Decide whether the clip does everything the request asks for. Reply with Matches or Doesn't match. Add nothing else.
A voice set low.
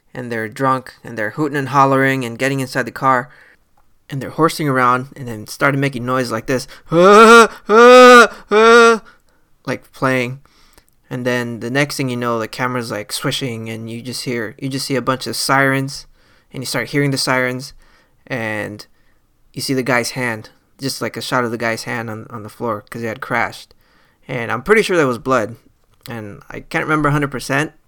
Matches